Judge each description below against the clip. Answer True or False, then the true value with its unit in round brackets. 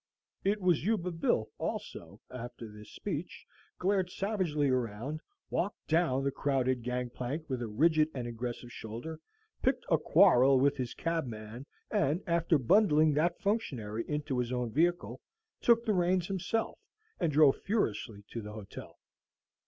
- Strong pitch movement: True (6.2 semitones)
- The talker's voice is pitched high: False (145 Hz)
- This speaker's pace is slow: False (145 wpm)